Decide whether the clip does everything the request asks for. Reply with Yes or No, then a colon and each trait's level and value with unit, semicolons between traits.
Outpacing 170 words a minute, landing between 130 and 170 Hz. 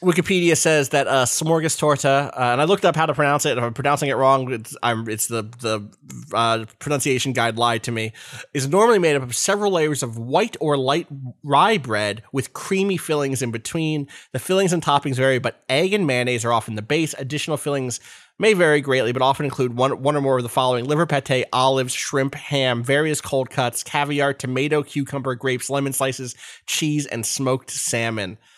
Yes: average, 195 wpm; low, 135 Hz